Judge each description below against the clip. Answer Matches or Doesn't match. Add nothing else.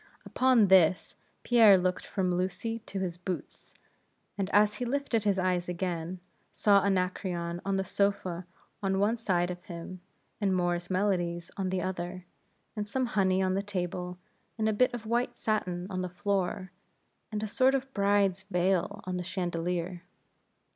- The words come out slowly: Doesn't match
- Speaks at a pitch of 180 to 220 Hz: Matches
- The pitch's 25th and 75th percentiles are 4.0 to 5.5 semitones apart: Doesn't match